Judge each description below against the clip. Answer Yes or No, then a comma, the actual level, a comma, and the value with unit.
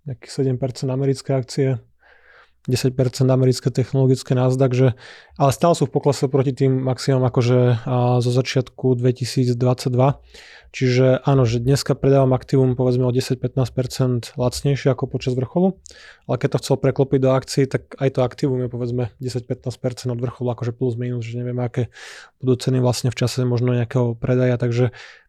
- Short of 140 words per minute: No, average, 155 wpm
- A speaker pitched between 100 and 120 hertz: No, low, 130 Hz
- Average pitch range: No, narrow, 1.4 semitones